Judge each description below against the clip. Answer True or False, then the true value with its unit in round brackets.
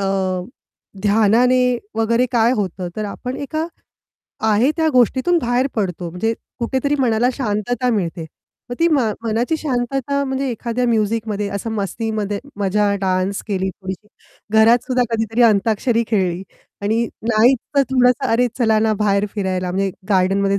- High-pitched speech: True (225 Hz)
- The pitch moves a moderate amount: True (3.8 semitones)